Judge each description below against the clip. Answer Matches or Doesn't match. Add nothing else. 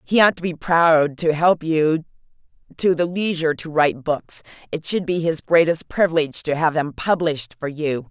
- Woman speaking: Matches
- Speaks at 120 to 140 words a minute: Doesn't match